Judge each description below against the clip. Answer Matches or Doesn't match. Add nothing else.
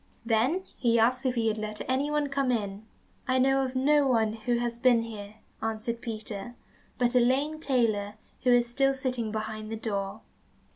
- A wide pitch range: Doesn't match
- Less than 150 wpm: Doesn't match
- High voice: Matches